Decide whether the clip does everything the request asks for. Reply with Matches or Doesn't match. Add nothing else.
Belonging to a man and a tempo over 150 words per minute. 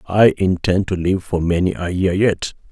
Matches